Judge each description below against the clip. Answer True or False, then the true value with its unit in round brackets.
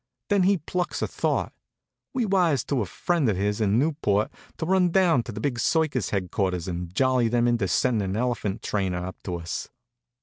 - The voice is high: False (120 Hz)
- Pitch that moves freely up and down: True (8.6 semitones)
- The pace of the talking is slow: False (195 wpm)